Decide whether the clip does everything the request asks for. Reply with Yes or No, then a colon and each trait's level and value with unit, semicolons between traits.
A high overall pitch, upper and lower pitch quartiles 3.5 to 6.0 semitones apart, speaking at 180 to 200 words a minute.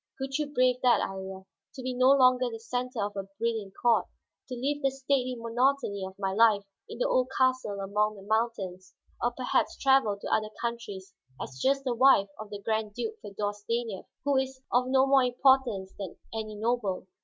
Yes: high, 235 Hz; average, 4.1 semitones; average, 190 wpm